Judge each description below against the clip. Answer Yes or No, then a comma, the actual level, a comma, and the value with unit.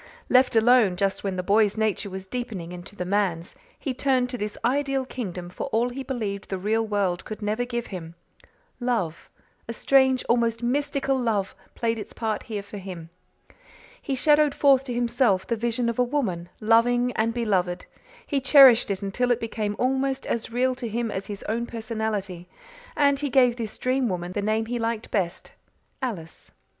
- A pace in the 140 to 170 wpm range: No, average, 180 wpm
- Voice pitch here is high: Yes, high, 230 Hz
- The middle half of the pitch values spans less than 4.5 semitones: Yes, average, 4.0 semitones